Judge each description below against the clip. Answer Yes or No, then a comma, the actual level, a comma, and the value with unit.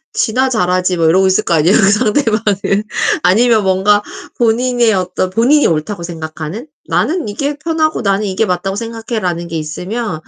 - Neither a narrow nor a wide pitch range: Yes, average, 4.3 semitones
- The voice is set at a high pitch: Yes, high, 205 Hz